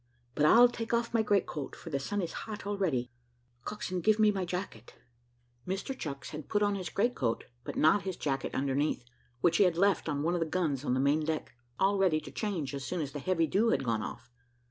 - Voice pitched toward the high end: No, medium, 170 Hz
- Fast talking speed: Yes, fast, 235 wpm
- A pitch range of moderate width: No, wide, 6.0 semitones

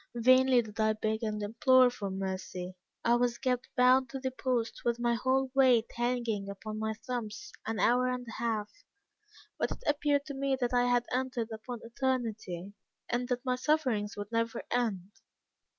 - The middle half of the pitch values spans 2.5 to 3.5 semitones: Yes, average, 2.8 semitones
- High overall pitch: Yes, high, 240 Hz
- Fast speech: No, average, 175 wpm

